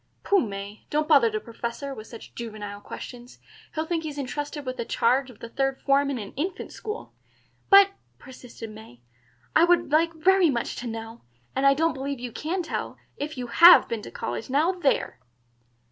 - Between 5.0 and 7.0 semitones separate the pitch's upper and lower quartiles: Yes, average, 5.3 semitones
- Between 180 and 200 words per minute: Yes, average, 190 wpm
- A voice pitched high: Yes, very high, 270 Hz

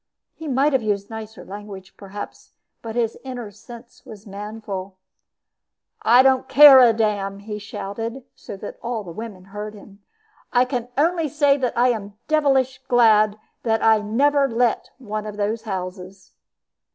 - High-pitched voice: Yes, high, 220 Hz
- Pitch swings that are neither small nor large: Yes, average, 3.7 semitones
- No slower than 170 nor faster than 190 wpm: No, average, 150 wpm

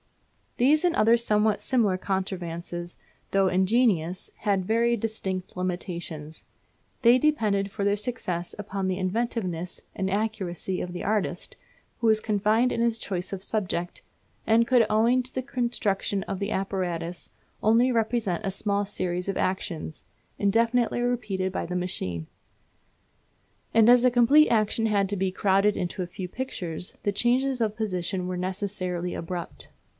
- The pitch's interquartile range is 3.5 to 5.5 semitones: Yes, average, 3.8 semitones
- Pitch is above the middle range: Yes, high, 200 Hz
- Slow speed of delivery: No, average, 150 wpm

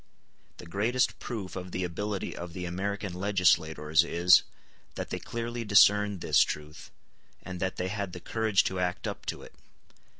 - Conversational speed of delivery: Yes, average, 165 wpm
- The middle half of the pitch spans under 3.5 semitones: Yes, average, 2.7 semitones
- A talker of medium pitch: No, very low, 95 Hz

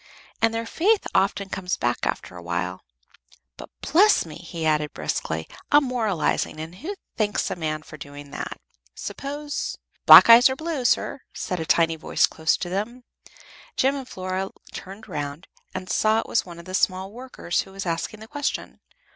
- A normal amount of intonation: No, wide, 7.4 semitones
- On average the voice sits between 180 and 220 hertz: Yes, high, 190 Hz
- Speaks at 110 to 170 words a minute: No, average, 180 wpm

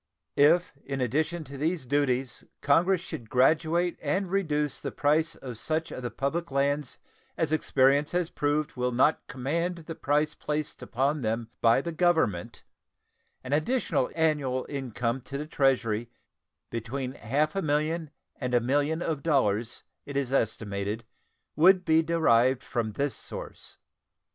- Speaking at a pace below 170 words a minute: Yes, average, 150 wpm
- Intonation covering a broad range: No, average, 4.0 semitones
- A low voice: No, medium, 145 Hz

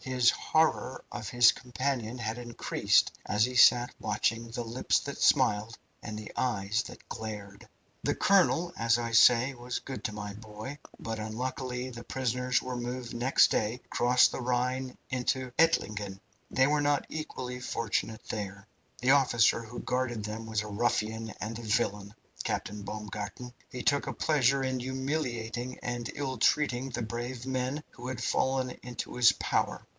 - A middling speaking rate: Yes, average, 160 wpm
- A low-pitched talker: Yes, low, 120 Hz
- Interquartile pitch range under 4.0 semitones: Yes, narrow, 2.6 semitones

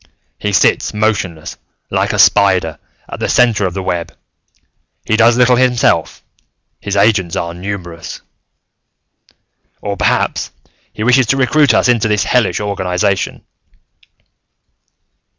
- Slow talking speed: Yes, slow, 120 wpm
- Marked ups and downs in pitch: No, average, 4.2 semitones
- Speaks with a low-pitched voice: Yes, low, 105 Hz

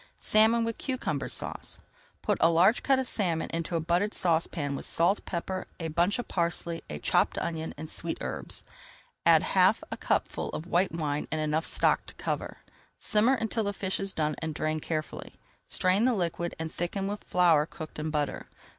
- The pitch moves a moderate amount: Yes, average, 4.0 semitones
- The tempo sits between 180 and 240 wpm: Yes, average, 185 wpm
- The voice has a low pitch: No, medium, 170 Hz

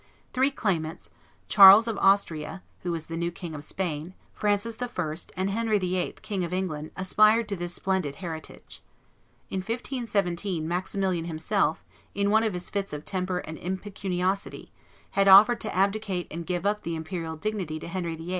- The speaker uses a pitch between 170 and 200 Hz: Yes, medium, 185 Hz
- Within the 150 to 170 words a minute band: Yes, average, 165 wpm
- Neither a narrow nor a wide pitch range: Yes, average, 3.2 semitones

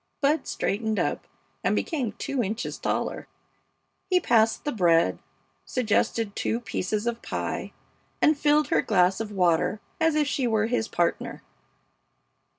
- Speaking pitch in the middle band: No, high, 225 Hz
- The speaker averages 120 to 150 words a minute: Yes, average, 140 wpm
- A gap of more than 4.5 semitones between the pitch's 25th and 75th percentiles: Yes, average, 5.2 semitones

